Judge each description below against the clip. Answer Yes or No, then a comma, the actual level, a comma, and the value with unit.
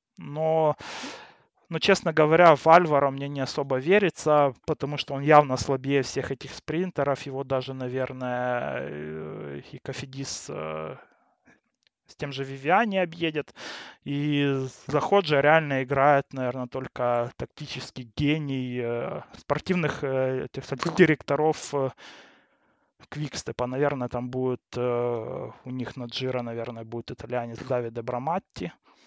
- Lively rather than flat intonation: No, average, 3.1 semitones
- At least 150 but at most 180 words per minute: No, average, 115 wpm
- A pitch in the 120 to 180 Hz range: Yes, low, 135 Hz